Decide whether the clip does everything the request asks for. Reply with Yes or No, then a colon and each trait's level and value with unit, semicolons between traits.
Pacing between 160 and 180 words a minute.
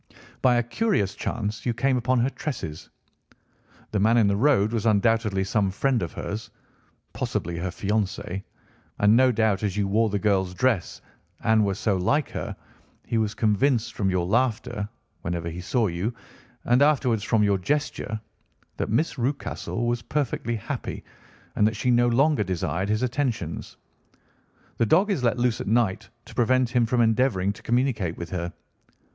Yes: average, 165 wpm